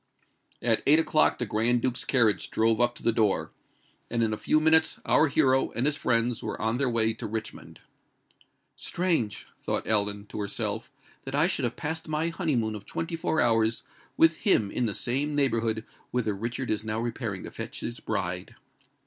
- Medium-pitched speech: No, low, 120 Hz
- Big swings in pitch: No, average, 4.9 semitones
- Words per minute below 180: No, average, 185 wpm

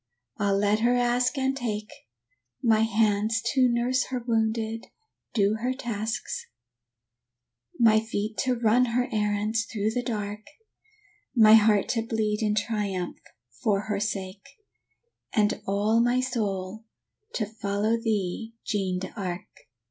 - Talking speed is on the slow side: Yes, slow, 125 wpm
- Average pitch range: No, narrow, 2.3 semitones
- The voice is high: Yes, high, 220 Hz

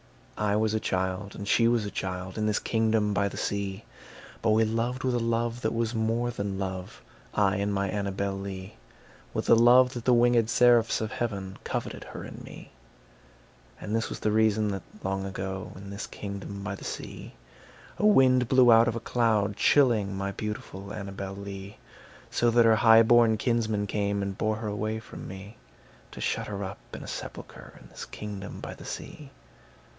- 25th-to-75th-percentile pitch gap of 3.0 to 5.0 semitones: No, narrow, 2.6 semitones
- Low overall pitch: Yes, low, 105 Hz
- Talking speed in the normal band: Yes, average, 190 wpm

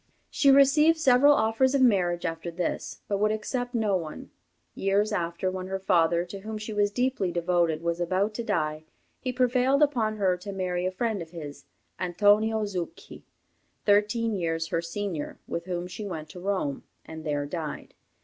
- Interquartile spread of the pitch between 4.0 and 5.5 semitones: Yes, average, 4.4 semitones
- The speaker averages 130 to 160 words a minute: No, average, 175 wpm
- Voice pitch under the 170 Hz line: No, high, 195 Hz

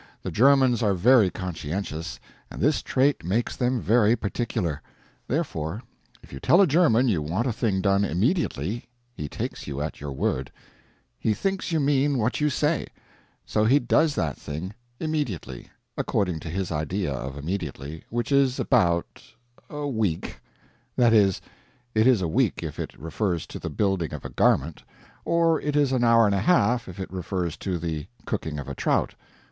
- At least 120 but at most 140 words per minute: No, average, 175 wpm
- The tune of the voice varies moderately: No, wide, 7.6 semitones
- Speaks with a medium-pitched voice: No, low, 105 Hz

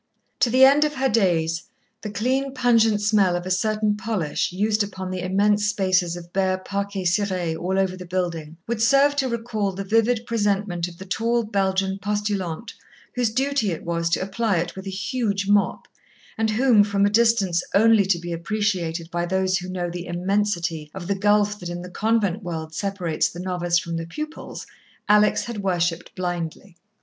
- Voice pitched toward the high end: Yes, high, 195 Hz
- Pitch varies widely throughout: No, average, 3.4 semitones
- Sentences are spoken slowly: No, average, 185 wpm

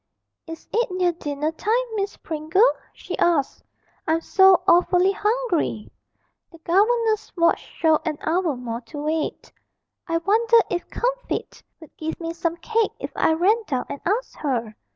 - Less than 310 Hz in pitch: No, very high, 340 Hz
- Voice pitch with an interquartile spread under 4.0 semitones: No, average, 4.9 semitones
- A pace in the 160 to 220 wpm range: No, average, 150 wpm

